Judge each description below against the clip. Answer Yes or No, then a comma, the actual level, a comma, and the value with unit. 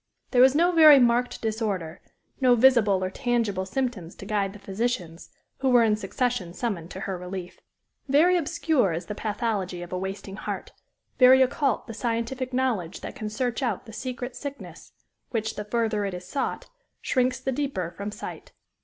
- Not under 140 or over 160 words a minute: No, average, 175 wpm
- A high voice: Yes, high, 225 Hz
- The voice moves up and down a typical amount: Yes, average, 4.8 semitones